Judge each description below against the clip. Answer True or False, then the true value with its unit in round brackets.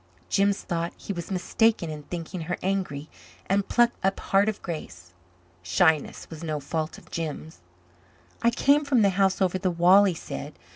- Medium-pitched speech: True (180 Hz)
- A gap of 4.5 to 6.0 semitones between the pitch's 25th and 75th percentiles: False (3.7 semitones)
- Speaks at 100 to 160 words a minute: False (175 wpm)